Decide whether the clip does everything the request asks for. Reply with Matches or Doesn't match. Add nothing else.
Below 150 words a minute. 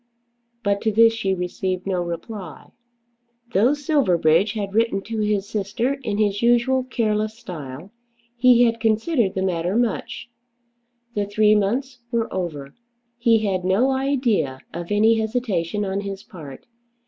Matches